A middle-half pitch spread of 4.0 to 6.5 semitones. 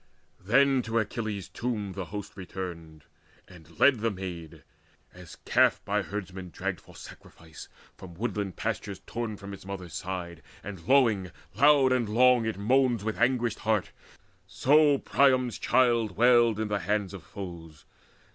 Yes: average, 4.4 semitones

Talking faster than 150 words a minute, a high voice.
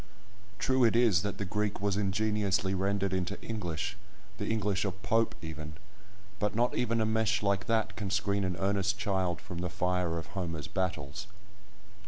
No: average, 170 wpm; low, 100 Hz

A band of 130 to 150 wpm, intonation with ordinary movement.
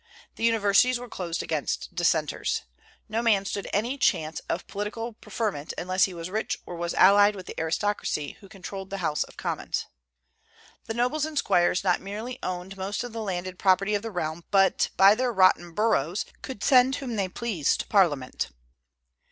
No: average, 175 wpm; average, 4.1 semitones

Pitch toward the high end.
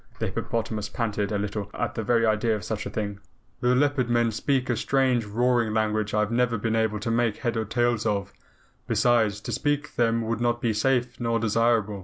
No: low, 115 Hz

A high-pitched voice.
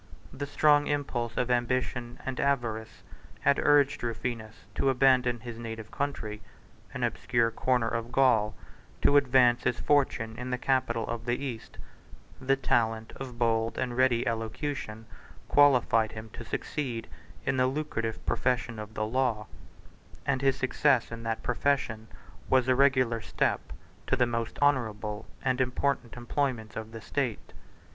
No: low, 120 Hz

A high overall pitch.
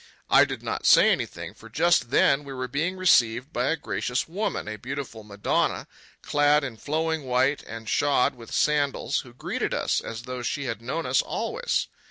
No: low, 135 Hz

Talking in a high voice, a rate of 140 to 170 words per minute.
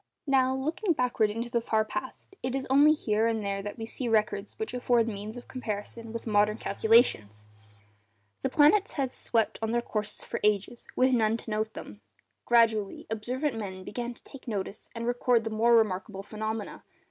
No: high, 225 Hz; average, 180 wpm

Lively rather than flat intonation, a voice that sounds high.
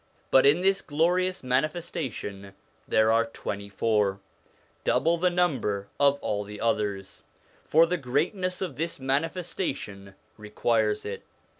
No: wide, 8.3 semitones; low, 130 Hz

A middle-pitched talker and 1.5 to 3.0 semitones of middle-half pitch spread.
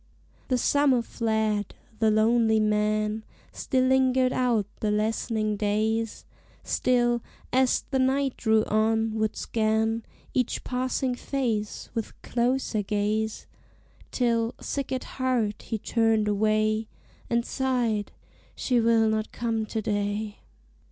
No: high, 225 Hz; narrow, 2.5 semitones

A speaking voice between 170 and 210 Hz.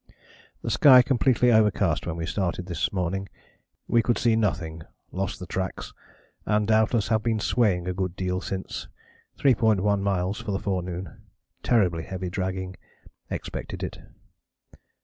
No: very low, 95 Hz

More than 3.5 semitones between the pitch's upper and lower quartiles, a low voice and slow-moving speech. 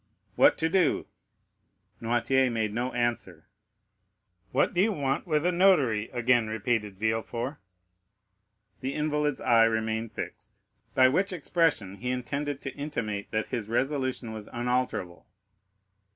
Yes: average, 4.6 semitones; low, 125 Hz; slow, 125 wpm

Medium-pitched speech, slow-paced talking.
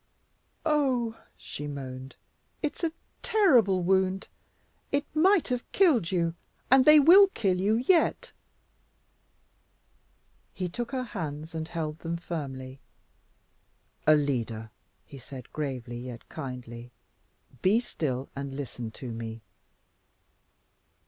Yes: medium, 165 Hz; slow, 110 wpm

